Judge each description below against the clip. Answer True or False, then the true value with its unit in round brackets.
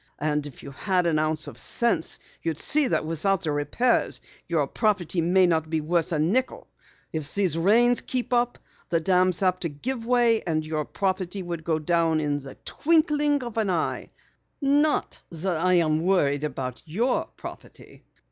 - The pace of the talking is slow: False (165 wpm)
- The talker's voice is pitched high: False (175 Hz)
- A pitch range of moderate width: False (6.3 semitones)